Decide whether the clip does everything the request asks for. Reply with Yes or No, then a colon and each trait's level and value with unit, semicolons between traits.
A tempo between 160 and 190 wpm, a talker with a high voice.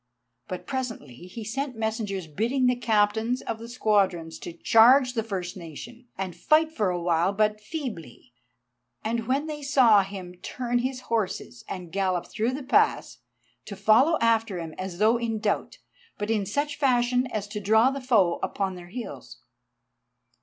Yes: average, 165 wpm; high, 220 Hz